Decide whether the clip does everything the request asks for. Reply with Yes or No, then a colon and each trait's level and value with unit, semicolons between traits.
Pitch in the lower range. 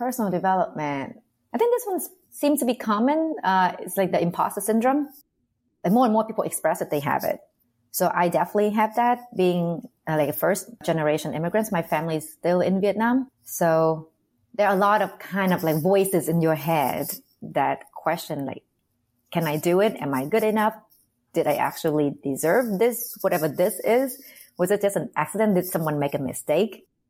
No: medium, 185 Hz